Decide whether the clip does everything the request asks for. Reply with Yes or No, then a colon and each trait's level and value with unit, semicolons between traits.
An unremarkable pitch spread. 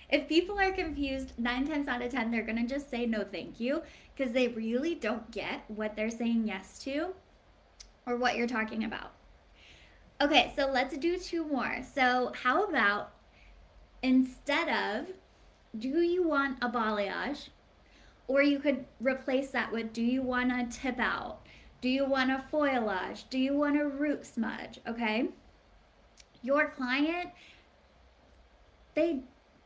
Yes: average, 3.8 semitones